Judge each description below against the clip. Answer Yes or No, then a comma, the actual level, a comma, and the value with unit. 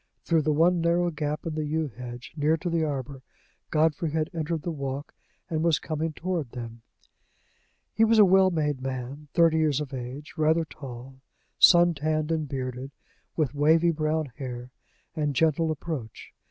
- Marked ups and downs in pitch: No, average, 3.1 semitones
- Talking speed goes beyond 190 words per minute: No, average, 165 wpm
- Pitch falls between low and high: Yes, medium, 155 Hz